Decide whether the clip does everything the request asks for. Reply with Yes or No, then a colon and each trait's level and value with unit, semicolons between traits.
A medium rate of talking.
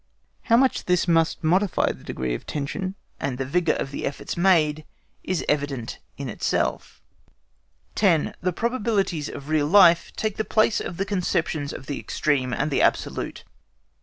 Yes: average, 165 wpm